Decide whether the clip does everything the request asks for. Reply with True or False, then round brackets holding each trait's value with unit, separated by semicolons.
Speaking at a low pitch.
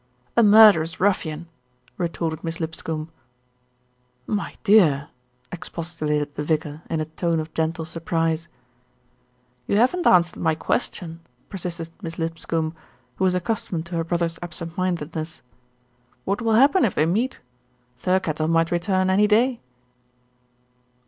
False (170 Hz)